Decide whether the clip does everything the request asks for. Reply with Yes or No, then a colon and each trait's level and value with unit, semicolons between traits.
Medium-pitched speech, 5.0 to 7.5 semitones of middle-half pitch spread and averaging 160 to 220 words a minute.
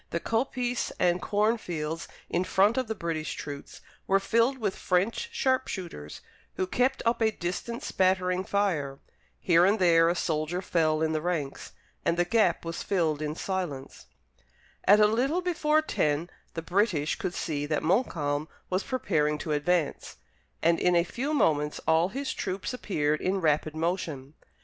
Yes: medium, 180 Hz; average, 5.3 semitones; average, 165 wpm